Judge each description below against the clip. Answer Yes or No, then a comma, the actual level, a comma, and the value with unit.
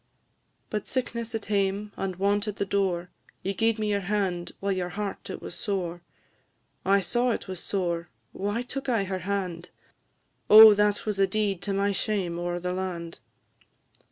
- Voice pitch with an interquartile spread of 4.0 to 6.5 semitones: No, narrow, 2.5 semitones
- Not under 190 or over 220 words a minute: No, average, 175 wpm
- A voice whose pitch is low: No, high, 195 Hz